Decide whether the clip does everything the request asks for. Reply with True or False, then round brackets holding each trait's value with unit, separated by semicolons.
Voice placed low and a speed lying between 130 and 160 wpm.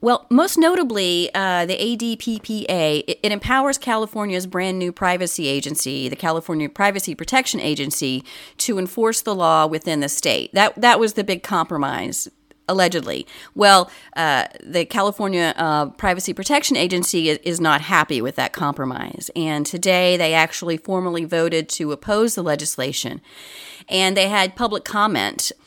False (180 Hz; 145 wpm)